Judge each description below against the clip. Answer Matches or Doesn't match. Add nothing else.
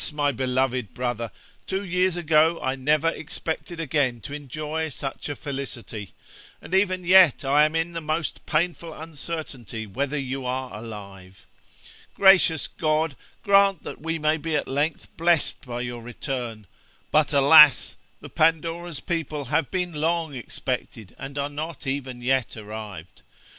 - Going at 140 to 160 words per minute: Matches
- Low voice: Doesn't match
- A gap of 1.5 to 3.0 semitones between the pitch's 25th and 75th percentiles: Doesn't match